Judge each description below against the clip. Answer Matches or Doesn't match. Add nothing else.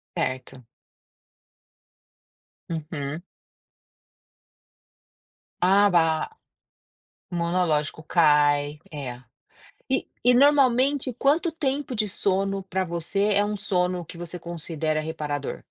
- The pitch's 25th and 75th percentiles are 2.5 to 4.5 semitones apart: Doesn't match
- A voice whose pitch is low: Doesn't match